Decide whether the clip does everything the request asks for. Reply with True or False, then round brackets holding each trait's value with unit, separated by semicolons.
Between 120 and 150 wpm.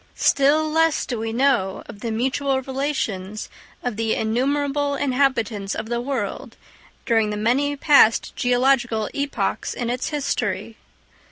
True (135 wpm)